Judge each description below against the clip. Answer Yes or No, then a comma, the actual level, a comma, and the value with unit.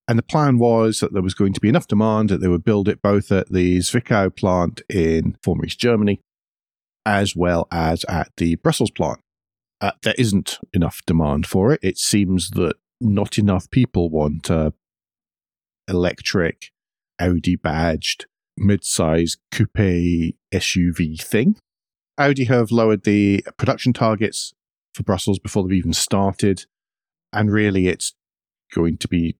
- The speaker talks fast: No, average, 150 wpm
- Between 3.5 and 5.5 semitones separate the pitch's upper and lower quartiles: Yes, average, 3.8 semitones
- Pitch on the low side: Yes, very low, 95 Hz